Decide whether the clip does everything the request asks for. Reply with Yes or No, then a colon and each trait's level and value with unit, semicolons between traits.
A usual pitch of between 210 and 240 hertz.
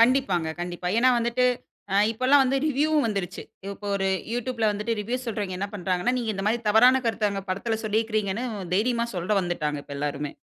Yes: high, 215 Hz